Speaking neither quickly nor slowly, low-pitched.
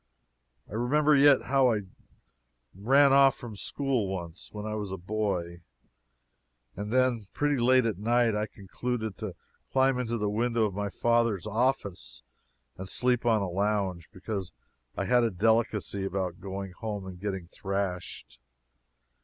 Yes: average, 145 wpm; low, 110 Hz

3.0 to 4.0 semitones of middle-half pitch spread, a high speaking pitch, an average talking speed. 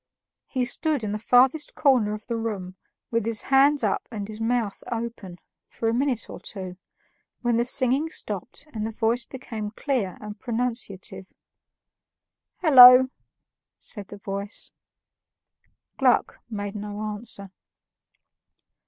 No: average, 3.3 semitones; high, 225 Hz; slow, 130 wpm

